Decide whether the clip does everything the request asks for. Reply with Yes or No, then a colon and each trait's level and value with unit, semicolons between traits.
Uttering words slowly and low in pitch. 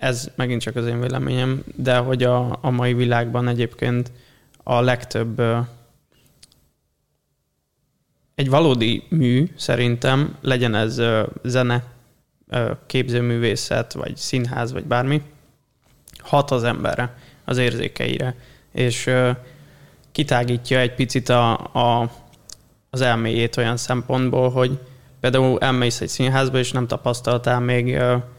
Yes: slow, 120 wpm; low, 125 Hz